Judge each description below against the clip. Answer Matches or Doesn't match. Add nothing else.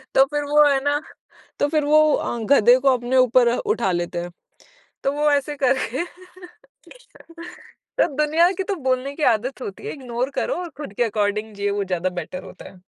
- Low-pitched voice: Doesn't match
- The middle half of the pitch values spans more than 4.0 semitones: Matches